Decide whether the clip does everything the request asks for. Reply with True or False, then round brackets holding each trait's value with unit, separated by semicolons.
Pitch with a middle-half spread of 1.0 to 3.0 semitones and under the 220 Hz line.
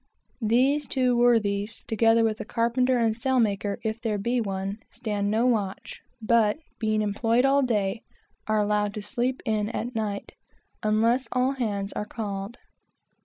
False (2.6 semitones; 225 Hz)